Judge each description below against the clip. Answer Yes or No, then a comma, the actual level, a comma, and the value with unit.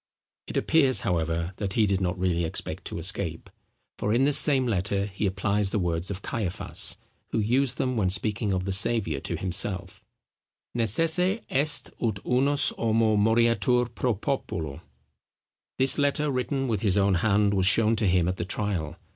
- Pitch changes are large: No, average, 4.7 semitones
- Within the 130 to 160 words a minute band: No, average, 170 wpm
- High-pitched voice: No, low, 105 Hz